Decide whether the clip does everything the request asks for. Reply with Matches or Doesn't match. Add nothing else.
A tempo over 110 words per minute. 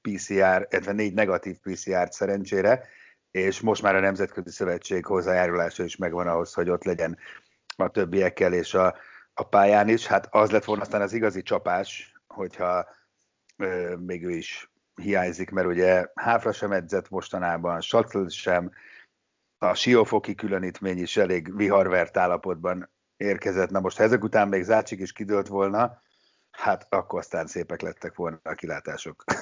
Matches